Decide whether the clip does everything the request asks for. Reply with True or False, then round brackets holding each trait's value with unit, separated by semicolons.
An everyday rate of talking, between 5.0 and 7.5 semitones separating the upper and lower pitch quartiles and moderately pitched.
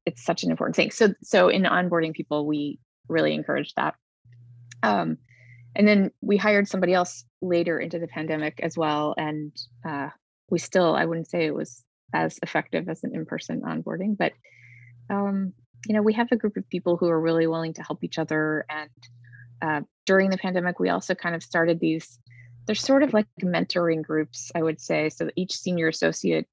True (190 wpm; 5.5 semitones; 165 Hz)